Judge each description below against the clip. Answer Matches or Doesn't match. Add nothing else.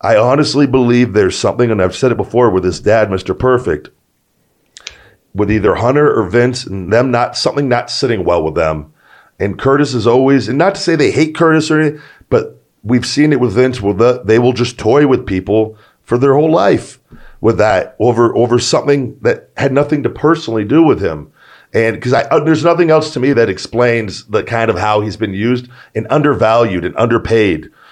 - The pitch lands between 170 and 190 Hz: Doesn't match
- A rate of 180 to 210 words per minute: Matches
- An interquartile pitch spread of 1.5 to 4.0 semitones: Doesn't match